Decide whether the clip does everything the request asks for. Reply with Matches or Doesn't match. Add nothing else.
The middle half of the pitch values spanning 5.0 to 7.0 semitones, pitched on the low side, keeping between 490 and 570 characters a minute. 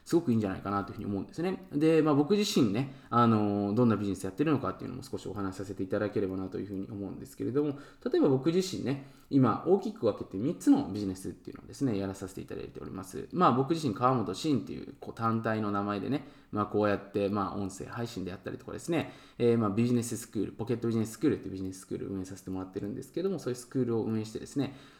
Matches